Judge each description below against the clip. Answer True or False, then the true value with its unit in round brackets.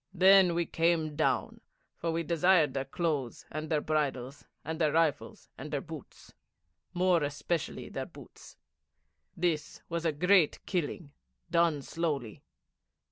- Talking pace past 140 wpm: False (135 wpm)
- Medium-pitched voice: True (160 Hz)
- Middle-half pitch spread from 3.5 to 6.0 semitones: False (2.8 semitones)